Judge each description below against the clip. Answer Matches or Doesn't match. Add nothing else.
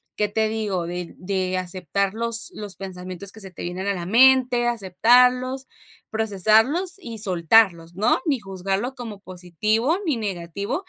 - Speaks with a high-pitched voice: Matches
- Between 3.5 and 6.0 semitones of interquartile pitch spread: Matches